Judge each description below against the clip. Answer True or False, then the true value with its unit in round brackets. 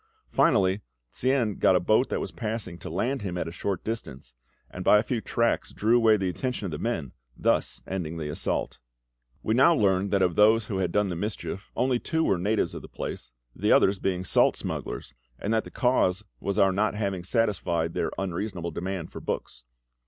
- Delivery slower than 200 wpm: False (205 wpm)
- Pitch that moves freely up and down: False (3.8 semitones)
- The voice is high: False (100 Hz)